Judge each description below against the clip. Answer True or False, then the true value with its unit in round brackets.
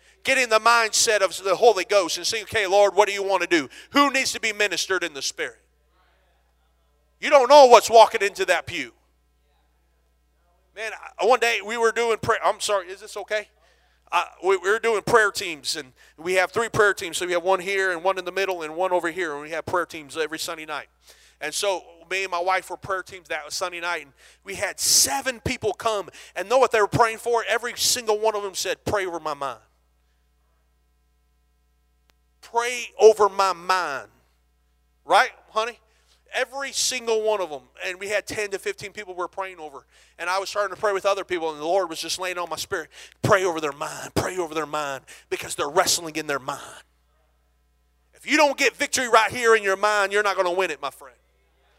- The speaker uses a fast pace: True (220 wpm)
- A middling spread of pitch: False (7.2 semitones)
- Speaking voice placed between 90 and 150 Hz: False (185 Hz)